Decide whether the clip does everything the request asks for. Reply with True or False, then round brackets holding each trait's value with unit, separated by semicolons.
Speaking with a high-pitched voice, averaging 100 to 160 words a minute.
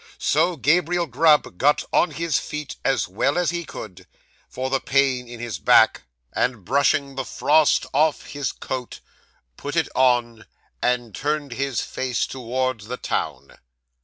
False (130 Hz; 150 wpm)